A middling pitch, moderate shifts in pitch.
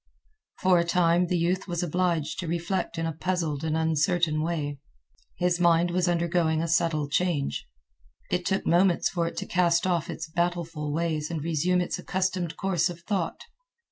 No: medium, 170 Hz; narrow, 1.8 semitones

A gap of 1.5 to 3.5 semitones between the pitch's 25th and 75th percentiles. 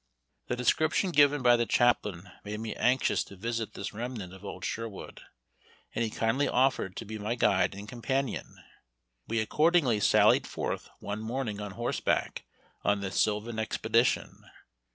Yes: average, 3.1 semitones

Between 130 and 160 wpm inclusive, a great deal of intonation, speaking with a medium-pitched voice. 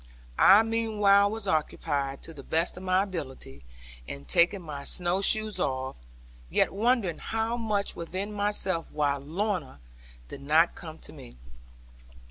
Yes: slow, 135 wpm; wide, 5.9 semitones; medium, 180 Hz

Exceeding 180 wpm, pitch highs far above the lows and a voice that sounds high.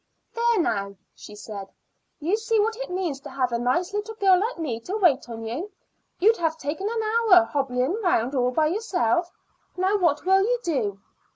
Yes: average, 190 wpm; wide, 8.6 semitones; very high, 345 Hz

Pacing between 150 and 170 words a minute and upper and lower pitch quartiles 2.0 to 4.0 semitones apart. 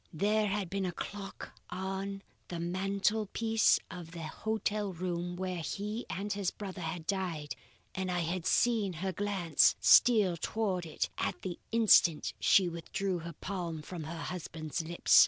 Yes: average, 155 wpm; average, 2.9 semitones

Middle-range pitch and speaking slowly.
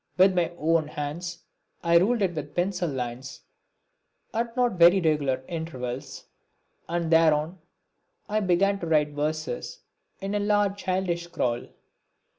Yes: medium, 170 Hz; slow, 130 wpm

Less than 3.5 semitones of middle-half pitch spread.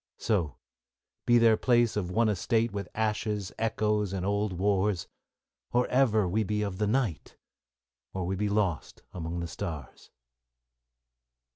Yes: average, 2.9 semitones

